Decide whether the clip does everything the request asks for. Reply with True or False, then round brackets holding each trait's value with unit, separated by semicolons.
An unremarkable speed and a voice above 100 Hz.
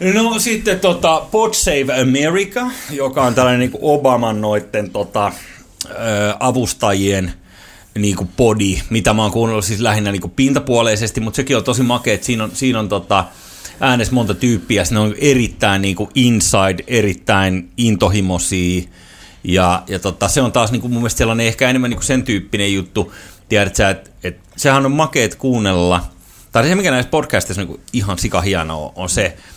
False (175 wpm; 110 Hz)